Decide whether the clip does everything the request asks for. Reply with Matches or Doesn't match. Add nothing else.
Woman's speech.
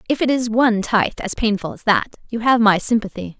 Matches